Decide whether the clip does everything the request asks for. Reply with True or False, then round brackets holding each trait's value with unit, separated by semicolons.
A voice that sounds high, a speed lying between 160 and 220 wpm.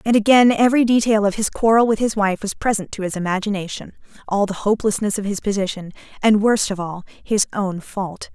True (205 Hz; 200 wpm)